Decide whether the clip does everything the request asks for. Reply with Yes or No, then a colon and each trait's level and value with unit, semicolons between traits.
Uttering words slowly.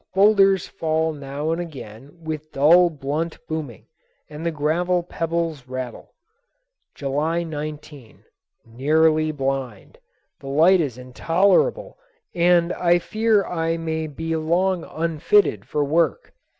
Yes: slow, 115 wpm